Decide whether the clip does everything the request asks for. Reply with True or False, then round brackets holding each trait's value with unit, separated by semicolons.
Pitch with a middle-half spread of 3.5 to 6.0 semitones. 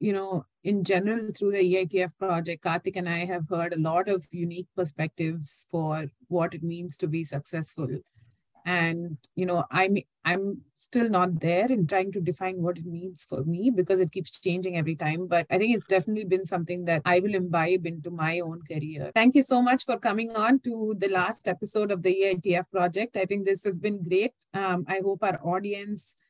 False (2.7 semitones)